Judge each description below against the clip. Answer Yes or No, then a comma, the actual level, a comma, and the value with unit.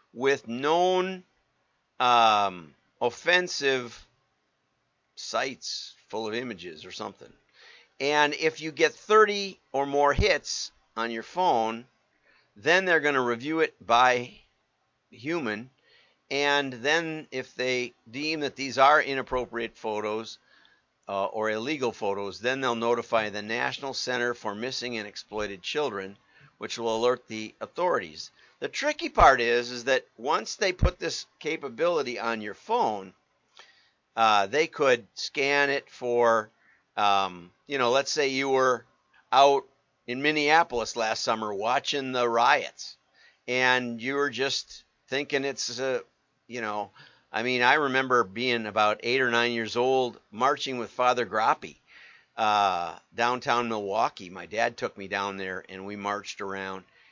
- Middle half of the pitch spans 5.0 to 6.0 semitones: No, average, 3.8 semitones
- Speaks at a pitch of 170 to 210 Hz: No, low, 125 Hz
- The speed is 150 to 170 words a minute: No, average, 140 wpm